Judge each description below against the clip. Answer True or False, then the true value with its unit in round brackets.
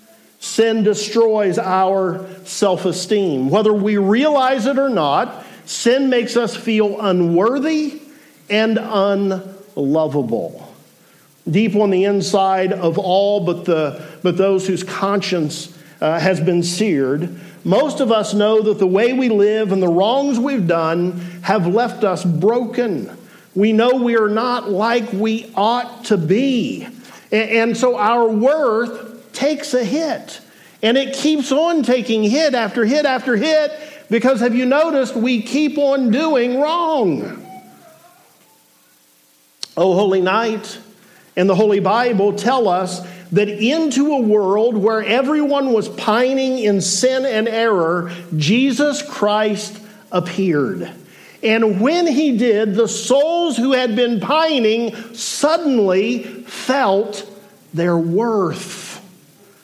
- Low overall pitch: False (220 Hz)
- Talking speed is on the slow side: True (130 wpm)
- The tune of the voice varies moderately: True (4.7 semitones)